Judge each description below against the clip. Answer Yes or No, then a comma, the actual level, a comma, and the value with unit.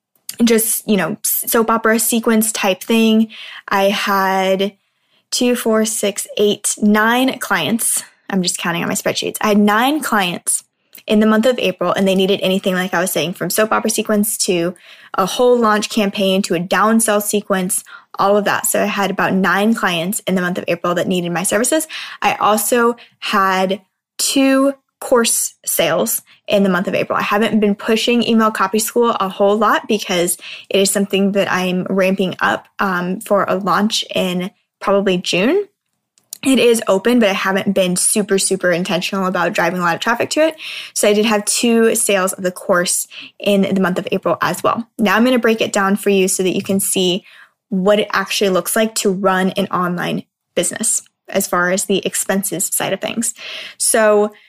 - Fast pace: No, average, 190 wpm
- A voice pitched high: Yes, high, 200 Hz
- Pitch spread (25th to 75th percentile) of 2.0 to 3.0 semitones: Yes, average, 2.7 semitones